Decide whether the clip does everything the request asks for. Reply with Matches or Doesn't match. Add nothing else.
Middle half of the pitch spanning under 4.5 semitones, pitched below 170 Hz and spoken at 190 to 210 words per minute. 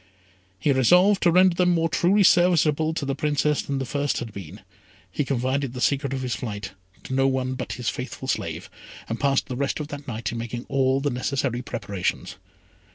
Matches